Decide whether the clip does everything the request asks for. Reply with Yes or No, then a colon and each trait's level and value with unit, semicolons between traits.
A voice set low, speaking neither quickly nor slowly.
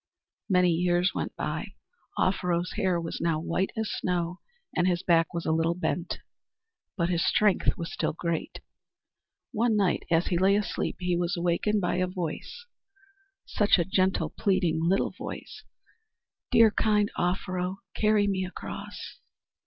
No: medium, 180 Hz; average, 150 wpm